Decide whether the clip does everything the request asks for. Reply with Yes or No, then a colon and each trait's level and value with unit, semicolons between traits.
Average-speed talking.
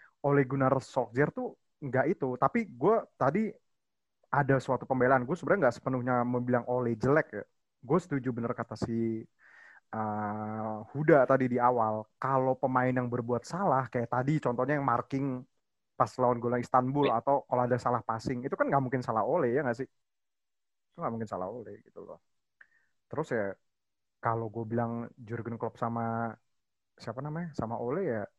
No: fast, 165 wpm